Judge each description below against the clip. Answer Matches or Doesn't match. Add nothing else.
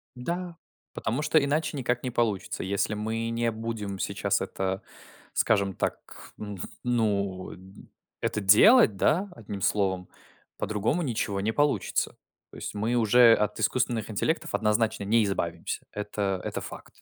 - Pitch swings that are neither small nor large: Matches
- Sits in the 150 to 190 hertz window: Doesn't match